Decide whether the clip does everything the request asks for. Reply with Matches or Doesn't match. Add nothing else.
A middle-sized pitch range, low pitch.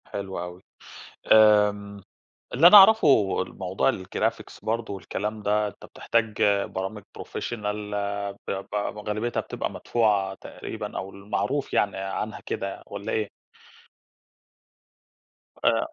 Doesn't match